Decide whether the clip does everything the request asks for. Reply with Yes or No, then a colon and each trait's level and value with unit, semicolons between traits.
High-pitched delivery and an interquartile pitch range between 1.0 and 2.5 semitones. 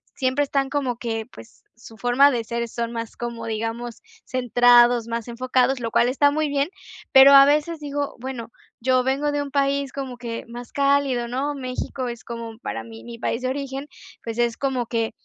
No: very high, 250 Hz; average, 2.9 semitones